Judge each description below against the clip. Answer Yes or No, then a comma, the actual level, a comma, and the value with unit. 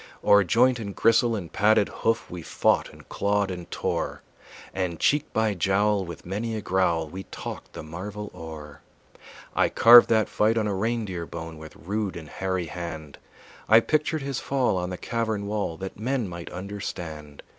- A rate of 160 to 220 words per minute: Yes, average, 175 wpm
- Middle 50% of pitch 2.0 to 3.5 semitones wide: No, average, 4.4 semitones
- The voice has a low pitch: Yes, low, 100 Hz